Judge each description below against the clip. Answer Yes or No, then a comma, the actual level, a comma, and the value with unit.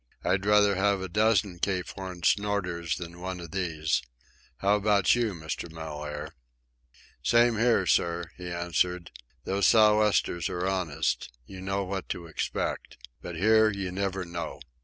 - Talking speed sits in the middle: Yes, average, 150 wpm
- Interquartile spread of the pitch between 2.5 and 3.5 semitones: Yes, average, 2.9 semitones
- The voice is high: No, very low, 95 Hz